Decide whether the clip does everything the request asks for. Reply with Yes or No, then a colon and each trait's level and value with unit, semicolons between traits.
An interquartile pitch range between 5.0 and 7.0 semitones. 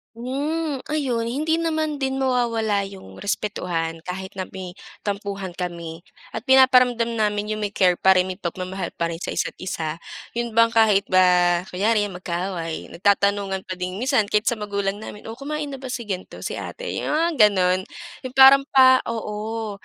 Yes: wide, 5.4 semitones